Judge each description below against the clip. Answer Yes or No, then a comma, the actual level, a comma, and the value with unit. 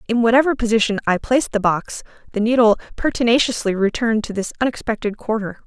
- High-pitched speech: Yes, high, 225 Hz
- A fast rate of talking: No, average, 160 wpm